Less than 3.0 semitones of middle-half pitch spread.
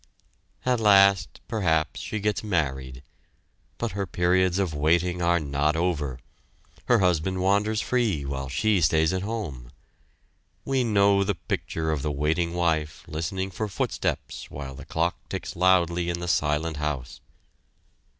No: average, 4.3 semitones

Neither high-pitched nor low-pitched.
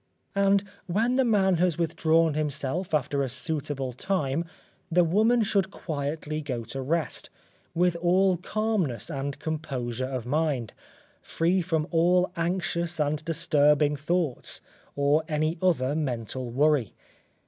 Yes: medium, 160 Hz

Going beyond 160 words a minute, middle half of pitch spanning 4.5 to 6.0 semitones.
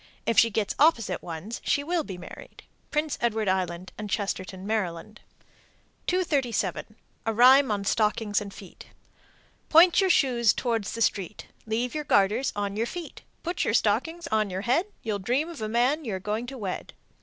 Yes: average, 175 wpm; average, 5.1 semitones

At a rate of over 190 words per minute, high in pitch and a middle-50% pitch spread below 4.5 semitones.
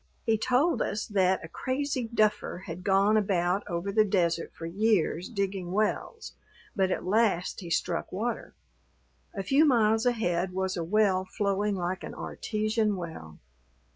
No: average, 150 wpm; high, 200 Hz; average, 3.2 semitones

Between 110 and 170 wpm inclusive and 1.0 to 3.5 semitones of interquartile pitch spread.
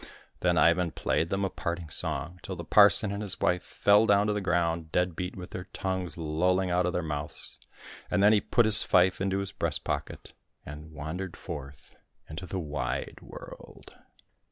No: average, 185 wpm; average, 3.2 semitones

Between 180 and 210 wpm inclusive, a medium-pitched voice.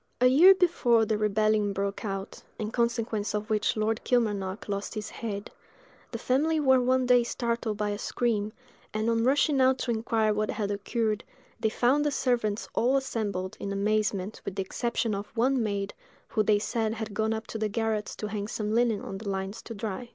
No: average, 195 wpm; high, 220 Hz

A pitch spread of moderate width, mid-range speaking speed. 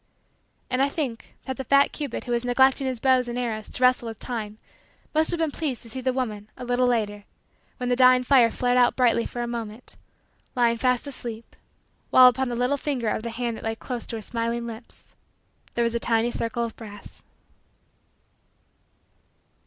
No: narrow, 1.9 semitones; average, 195 wpm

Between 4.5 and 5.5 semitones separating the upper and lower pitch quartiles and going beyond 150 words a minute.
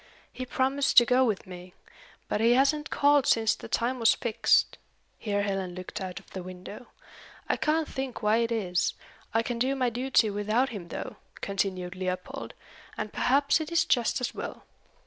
Yes: average, 5.0 semitones; average, 180 wpm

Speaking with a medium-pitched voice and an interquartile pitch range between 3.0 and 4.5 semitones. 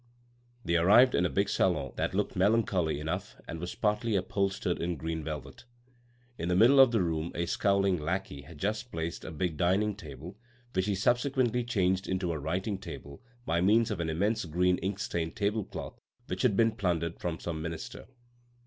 No: very low, 90 Hz; average, 4.1 semitones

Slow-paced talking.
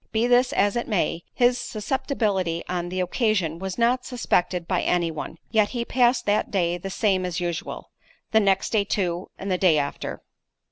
No: average, 180 wpm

